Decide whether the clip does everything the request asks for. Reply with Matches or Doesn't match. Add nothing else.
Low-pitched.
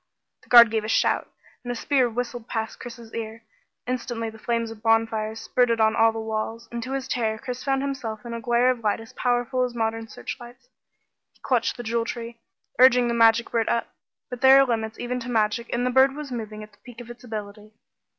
Doesn't match